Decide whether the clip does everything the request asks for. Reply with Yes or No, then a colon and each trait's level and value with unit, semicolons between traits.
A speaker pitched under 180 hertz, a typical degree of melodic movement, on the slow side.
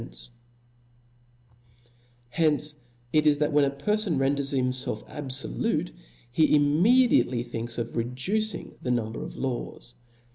Yes: medium, 140 Hz; average, 3.8 semitones; slow, 115 wpm